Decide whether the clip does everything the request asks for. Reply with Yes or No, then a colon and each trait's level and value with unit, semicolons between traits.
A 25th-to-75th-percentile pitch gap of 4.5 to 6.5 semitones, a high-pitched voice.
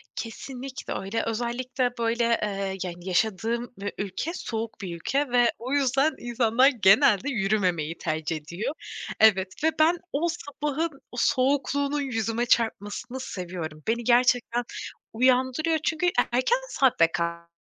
Yes: wide, 5.5 semitones; high, 235 Hz